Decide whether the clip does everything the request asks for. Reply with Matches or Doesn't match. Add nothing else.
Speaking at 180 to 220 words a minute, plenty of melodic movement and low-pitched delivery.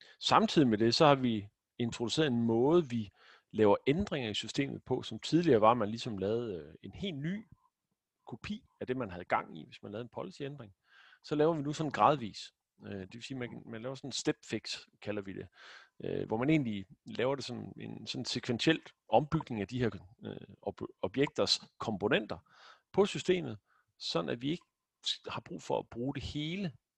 Matches